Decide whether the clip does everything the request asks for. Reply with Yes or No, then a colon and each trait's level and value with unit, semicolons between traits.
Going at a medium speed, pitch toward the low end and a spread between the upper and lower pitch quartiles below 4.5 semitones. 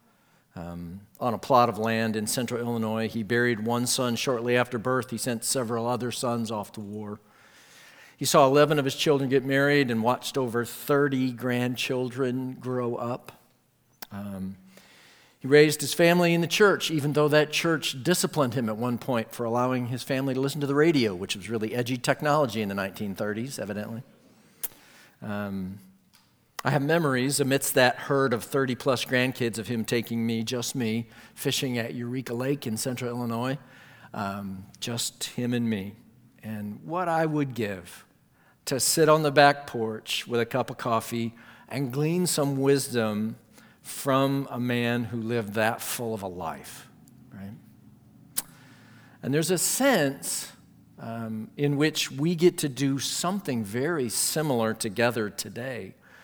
Yes: average, 160 wpm; low, 125 Hz; average, 3.6 semitones